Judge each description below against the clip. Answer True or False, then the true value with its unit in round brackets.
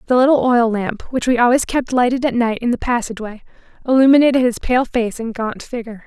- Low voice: False (240 Hz)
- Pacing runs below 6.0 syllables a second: False (6.1 syllables/s)